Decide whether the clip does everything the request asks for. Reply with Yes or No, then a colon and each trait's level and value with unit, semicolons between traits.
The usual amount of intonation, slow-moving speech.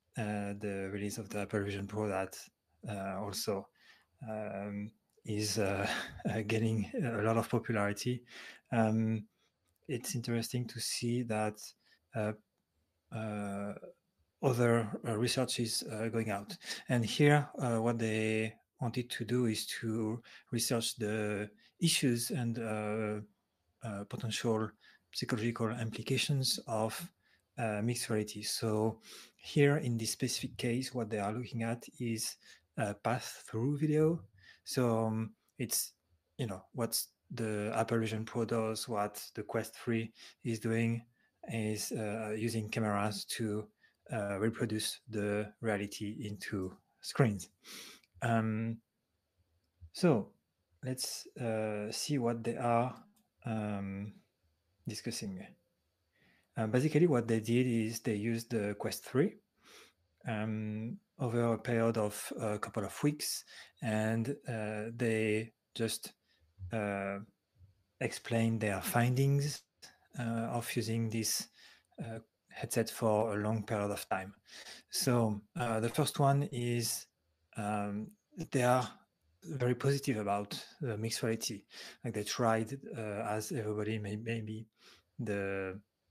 No: narrow, 2.1 semitones; slow, 125 wpm